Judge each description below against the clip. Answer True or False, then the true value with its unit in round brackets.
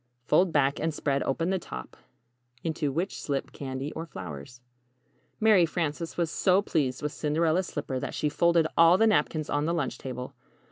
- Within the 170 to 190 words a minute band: True (180 wpm)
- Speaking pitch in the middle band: True (155 Hz)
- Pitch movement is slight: False (3.8 semitones)